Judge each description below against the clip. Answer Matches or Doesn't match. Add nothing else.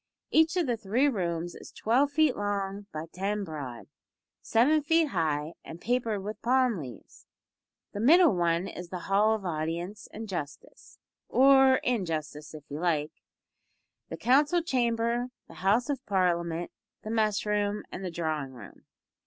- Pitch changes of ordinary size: Doesn't match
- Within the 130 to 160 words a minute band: Matches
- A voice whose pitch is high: Matches